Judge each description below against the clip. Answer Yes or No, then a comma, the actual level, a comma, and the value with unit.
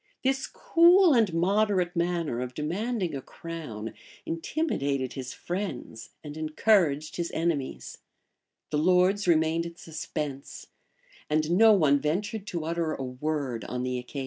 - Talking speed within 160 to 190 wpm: No, average, 140 wpm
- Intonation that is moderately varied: Yes, average, 4.8 semitones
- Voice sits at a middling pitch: Yes, medium, 165 Hz